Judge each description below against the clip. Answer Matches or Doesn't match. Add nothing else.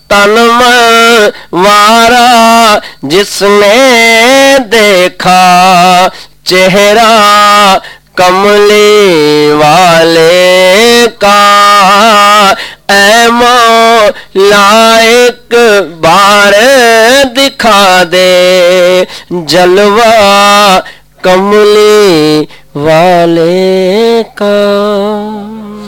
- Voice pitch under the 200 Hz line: Doesn't match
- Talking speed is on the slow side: Matches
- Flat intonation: Doesn't match